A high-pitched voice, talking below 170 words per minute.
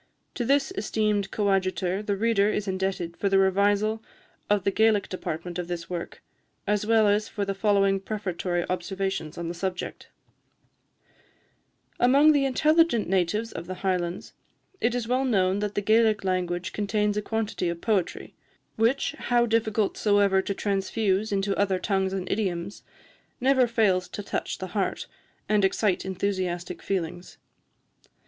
Yes: high, 200 Hz; average, 150 wpm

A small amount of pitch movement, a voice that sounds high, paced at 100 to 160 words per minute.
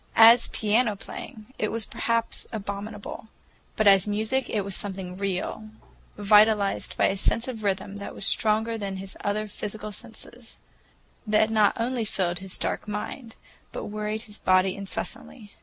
Yes: narrow, 1.8 semitones; high, 210 Hz; average, 150 wpm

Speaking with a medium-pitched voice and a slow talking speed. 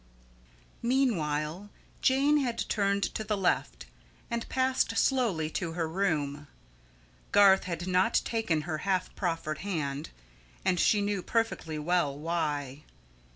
Yes: medium, 180 Hz; slow, 120 wpm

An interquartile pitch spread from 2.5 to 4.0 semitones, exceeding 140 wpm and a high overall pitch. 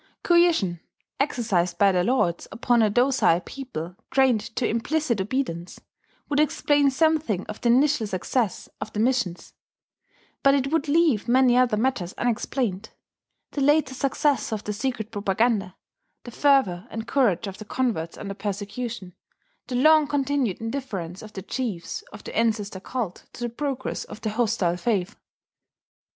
No: average, 5.1 semitones; average, 150 wpm; high, 235 Hz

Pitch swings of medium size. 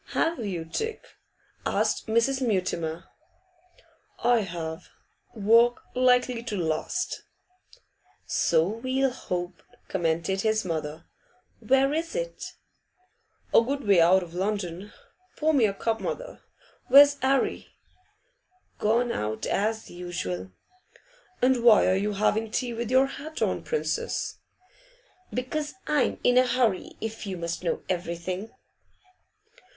No: wide, 6.2 semitones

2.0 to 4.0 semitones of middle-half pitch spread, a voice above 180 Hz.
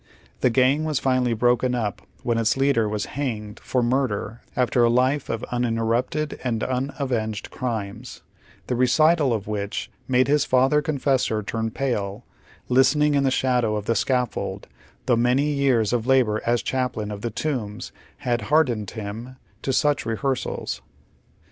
No: average, 3.0 semitones; low, 125 Hz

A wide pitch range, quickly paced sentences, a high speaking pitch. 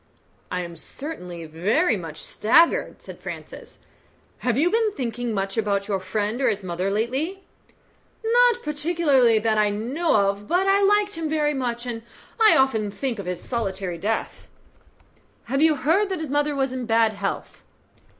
No: wide, 7.5 semitones; average, 165 wpm; high, 240 Hz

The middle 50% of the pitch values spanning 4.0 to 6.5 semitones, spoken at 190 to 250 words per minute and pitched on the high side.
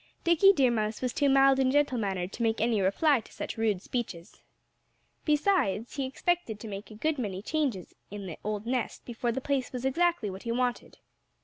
Yes: average, 4.8 semitones; average, 200 wpm; high, 240 Hz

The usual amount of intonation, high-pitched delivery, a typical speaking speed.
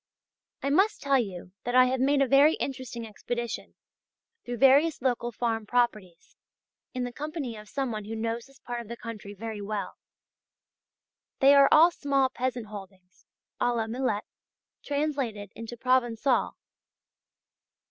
Yes: average, 3.6 semitones; high, 245 Hz; average, 145 wpm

